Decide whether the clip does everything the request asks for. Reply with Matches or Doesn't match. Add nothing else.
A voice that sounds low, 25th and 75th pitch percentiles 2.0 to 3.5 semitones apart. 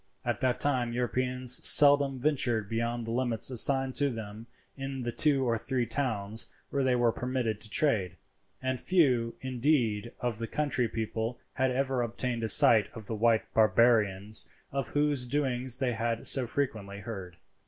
Matches